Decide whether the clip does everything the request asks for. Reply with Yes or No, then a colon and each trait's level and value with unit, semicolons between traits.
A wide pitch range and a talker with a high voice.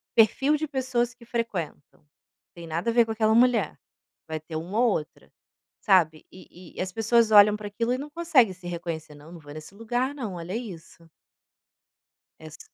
Yes: wide, 6.0 semitones; high, 210 Hz